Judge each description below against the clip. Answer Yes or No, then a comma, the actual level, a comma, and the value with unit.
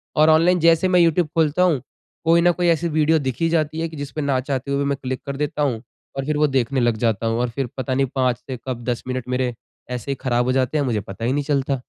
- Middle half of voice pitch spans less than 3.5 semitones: No, average, 3.8 semitones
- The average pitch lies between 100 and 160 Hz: Yes, medium, 140 Hz